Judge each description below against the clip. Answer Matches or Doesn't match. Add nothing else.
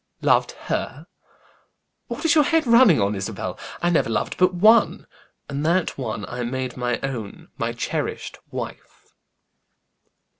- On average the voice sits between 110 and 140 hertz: Matches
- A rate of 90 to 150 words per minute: Matches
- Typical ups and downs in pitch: Doesn't match